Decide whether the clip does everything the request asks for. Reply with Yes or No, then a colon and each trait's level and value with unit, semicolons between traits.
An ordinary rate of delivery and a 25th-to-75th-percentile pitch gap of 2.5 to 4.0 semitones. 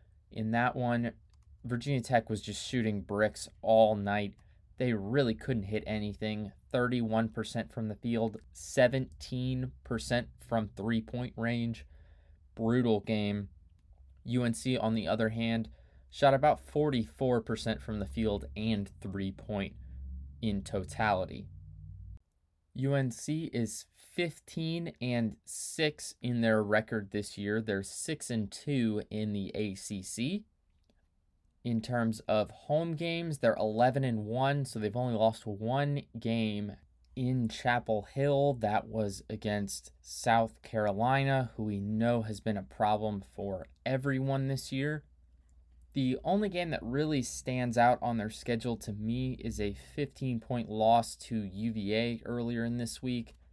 No: slow, 130 wpm; average, 3.4 semitones